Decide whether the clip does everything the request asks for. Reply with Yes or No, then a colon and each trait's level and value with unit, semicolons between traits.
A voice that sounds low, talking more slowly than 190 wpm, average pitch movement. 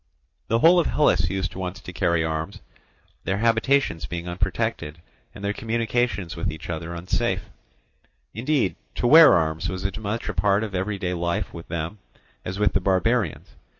Yes: very low, 95 Hz; average, 165 wpm; average, 4.5 semitones